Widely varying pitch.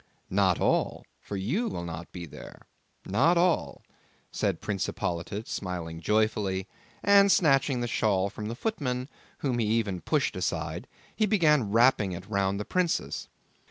Yes: wide, 7.0 semitones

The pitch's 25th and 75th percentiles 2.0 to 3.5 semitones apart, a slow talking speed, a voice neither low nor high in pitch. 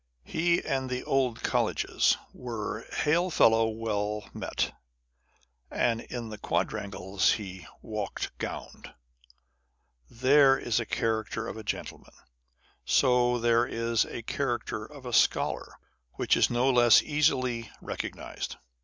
No: average, 2.8 semitones; slow, 130 wpm; low, 115 Hz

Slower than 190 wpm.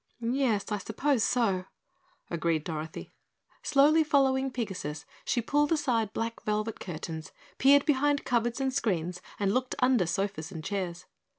Yes: slow, 135 wpm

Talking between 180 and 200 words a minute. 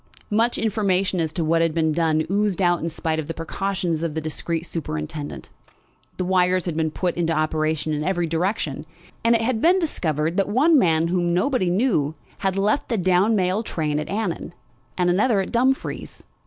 Yes: average, 190 wpm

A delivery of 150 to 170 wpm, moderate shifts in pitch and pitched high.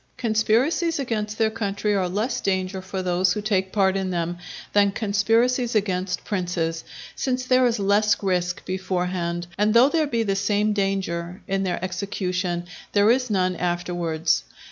Yes: average, 155 wpm; average, 3.0 semitones; high, 195 Hz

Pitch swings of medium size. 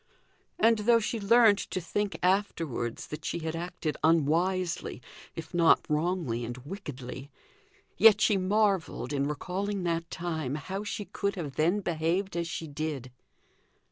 Yes: average, 4.6 semitones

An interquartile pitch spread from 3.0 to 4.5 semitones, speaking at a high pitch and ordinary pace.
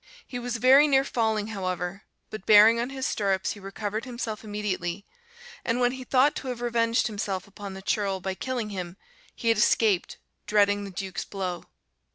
Yes: average, 3.5 semitones; high, 210 Hz; average, 180 wpm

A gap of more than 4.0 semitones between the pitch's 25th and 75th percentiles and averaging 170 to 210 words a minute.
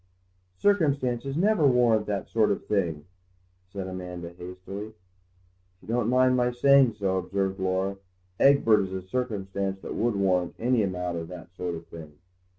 No: average, 5.1 semitones; average, 155 wpm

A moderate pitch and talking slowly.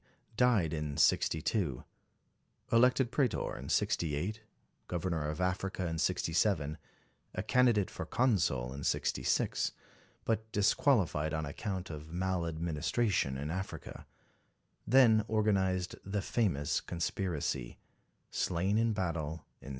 No: very low, 90 Hz; slow, 110 wpm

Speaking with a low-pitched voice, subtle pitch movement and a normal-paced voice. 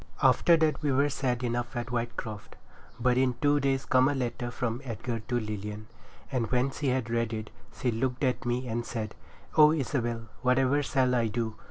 Yes: low, 125 Hz; narrow, 2.2 semitones; average, 190 wpm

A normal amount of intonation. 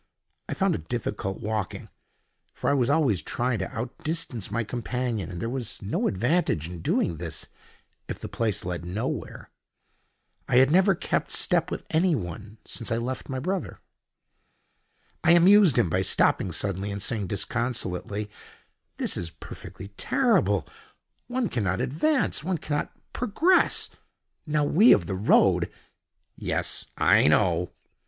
No: wide, 7.9 semitones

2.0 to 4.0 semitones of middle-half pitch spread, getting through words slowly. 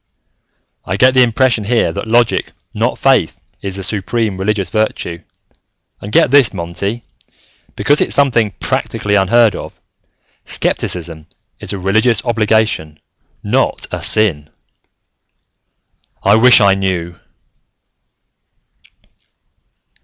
Yes: average, 3.6 semitones; slow, 110 wpm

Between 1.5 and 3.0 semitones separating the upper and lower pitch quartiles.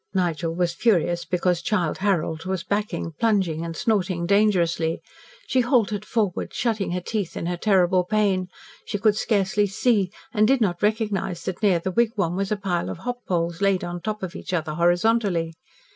No: average, 3.5 semitones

